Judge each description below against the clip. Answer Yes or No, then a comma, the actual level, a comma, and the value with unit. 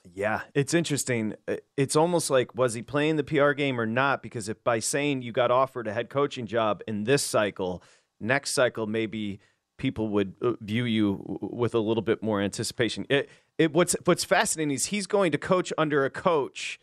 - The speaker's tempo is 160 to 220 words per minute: Yes, average, 195 wpm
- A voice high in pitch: No, low, 125 Hz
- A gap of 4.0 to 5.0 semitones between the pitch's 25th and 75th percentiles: Yes, average, 4.7 semitones